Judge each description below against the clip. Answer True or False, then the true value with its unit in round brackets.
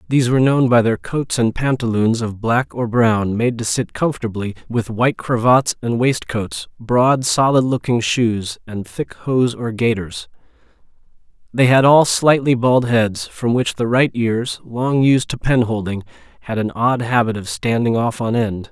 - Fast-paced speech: False (175 wpm)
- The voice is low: True (120 Hz)